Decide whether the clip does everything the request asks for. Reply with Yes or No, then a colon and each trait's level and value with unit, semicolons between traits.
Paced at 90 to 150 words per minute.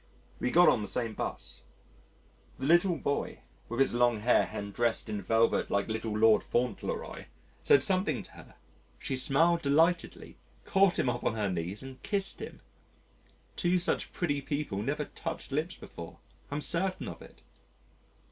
No: average, 160 wpm